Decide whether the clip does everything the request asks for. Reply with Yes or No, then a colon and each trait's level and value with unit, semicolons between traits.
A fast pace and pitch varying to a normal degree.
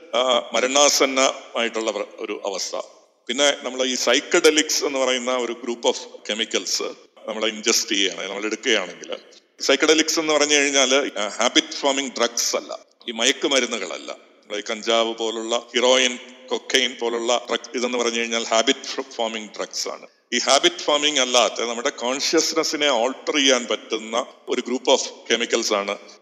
Yes: fast, 130 wpm; average, 4.1 semitones